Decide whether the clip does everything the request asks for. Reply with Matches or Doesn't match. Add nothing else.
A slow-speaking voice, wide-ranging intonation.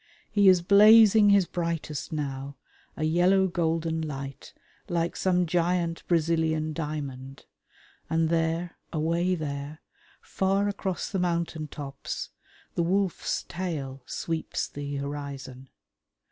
Doesn't match